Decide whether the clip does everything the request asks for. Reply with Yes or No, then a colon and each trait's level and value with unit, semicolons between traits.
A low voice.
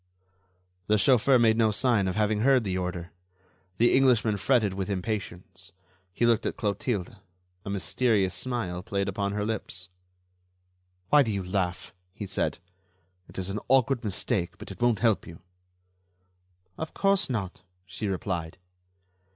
Yes: low, 105 Hz